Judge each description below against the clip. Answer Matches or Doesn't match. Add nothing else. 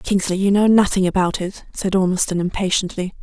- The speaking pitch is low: Doesn't match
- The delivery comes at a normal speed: Matches